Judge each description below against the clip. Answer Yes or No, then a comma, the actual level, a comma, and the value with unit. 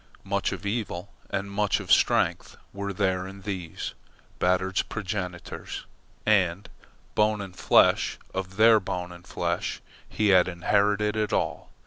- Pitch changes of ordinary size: No, narrow, 2.2 semitones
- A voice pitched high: No, low, 100 Hz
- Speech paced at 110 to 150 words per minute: Yes, slow, 135 wpm